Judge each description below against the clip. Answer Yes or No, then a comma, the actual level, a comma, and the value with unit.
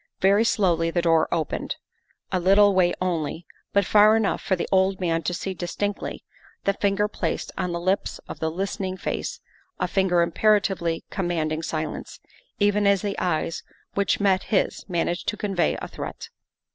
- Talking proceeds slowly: No, average, 165 wpm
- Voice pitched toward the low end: No, medium, 185 Hz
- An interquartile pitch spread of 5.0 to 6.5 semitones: No, average, 2.7 semitones